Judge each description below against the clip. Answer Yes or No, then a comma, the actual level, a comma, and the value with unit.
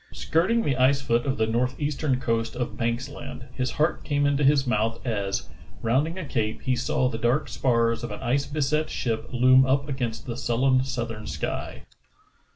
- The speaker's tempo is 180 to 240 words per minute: Yes, average, 185 wpm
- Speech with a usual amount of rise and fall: Yes, average, 3.1 semitones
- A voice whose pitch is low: Yes, low, 125 Hz